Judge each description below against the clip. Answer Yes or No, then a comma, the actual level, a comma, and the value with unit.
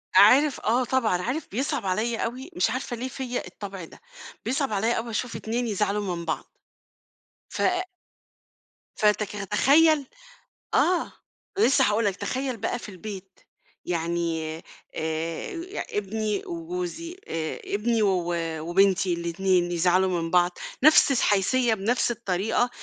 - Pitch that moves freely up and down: Yes, wide, 5.9 semitones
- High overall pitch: Yes, high, 210 Hz